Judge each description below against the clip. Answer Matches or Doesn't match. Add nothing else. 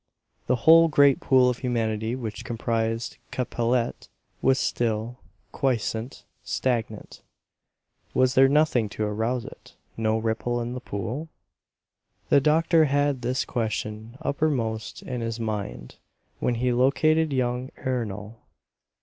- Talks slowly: Matches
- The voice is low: Matches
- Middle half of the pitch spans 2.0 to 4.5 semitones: Matches